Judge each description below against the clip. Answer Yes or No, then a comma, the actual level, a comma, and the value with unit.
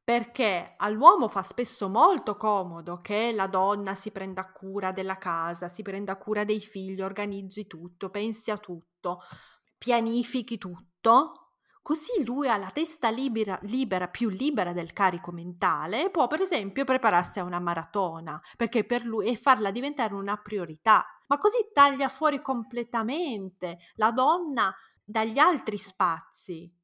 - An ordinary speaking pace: Yes, average, 145 wpm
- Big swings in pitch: No, average, 4.4 semitones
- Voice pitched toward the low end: No, high, 210 Hz